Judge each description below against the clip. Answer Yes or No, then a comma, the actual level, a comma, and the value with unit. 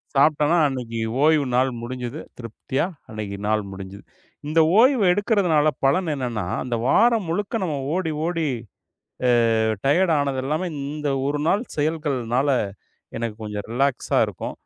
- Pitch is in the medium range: Yes, medium, 145 Hz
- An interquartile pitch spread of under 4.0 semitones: No, wide, 5.4 semitones